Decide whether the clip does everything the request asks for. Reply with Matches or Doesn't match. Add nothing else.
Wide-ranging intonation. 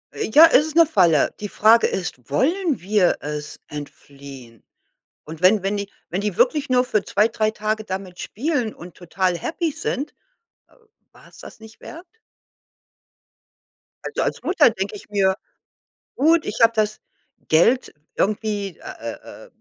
Matches